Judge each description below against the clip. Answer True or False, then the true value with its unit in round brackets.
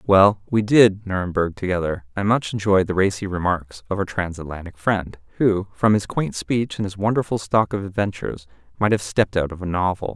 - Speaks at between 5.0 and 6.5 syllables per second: True (5.3 syllables/s)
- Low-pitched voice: True (95 Hz)